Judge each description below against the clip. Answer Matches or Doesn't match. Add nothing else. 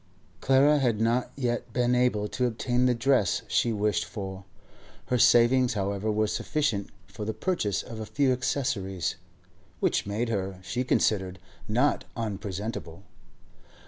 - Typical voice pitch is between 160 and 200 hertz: Doesn't match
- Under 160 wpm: Matches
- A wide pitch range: Doesn't match